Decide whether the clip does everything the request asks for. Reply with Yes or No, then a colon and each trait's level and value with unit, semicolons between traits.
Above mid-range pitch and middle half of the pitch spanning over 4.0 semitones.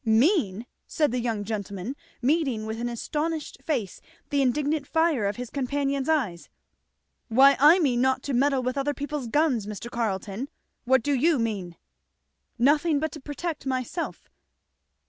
Yes: very high, 265 Hz; average, 4.4 semitones